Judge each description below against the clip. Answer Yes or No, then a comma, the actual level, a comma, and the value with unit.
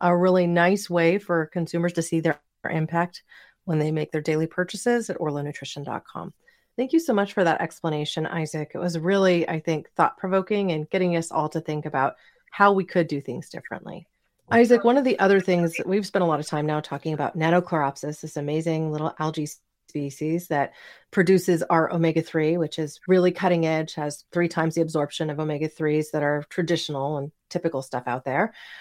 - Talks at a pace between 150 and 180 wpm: No, average, 195 wpm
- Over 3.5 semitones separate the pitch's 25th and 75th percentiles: No, average, 2.8 semitones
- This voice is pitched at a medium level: Yes, medium, 165 Hz